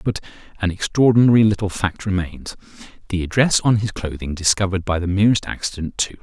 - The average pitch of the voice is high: No, low, 100 Hz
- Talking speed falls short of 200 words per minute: Yes, average, 165 wpm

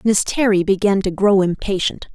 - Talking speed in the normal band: Yes, average, 170 wpm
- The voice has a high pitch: Yes, high, 200 Hz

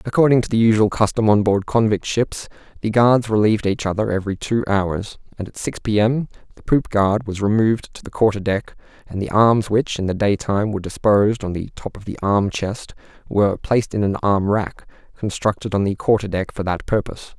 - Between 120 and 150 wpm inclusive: No, fast, 205 wpm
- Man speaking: Yes, male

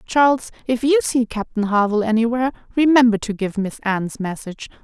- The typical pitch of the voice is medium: No, high, 230 Hz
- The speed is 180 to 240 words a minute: No, average, 160 wpm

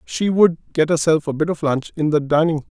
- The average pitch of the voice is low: No, medium, 160 Hz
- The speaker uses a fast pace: Yes, fast, 260 wpm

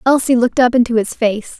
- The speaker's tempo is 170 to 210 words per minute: No, fast, 225 wpm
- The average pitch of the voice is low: No, high, 240 Hz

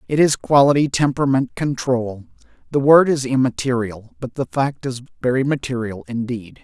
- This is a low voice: Yes, low, 130 Hz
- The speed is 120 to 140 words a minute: Yes, slow, 135 wpm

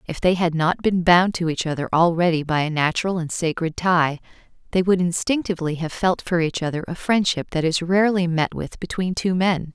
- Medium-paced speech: No, fast, 210 wpm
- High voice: No, medium, 170 Hz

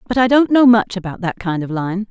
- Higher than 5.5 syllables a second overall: Yes, 5.7 syllables/s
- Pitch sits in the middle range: No, high, 205 Hz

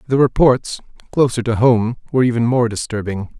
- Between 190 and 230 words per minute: No, average, 160 wpm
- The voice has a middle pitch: No, low, 120 Hz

